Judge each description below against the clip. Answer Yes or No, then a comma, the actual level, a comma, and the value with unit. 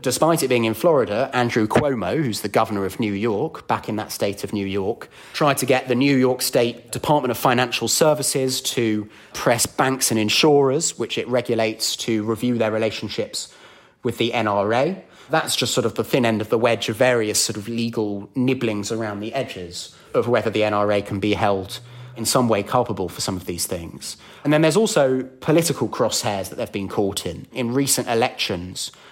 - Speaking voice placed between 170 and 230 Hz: No, low, 115 Hz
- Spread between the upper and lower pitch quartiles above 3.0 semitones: Yes, average, 3.4 semitones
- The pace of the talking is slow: No, average, 195 wpm